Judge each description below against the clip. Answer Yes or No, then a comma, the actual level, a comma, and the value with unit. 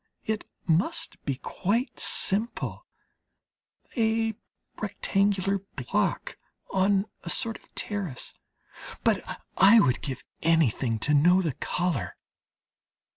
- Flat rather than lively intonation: No, average, 5.1 semitones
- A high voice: Yes, high, 195 Hz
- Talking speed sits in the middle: No, slow, 100 wpm